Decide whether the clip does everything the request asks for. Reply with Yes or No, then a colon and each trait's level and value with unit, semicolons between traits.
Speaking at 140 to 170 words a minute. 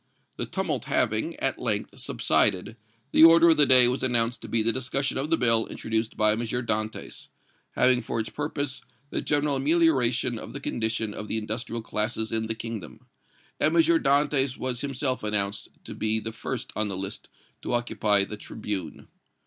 No: average, 180 wpm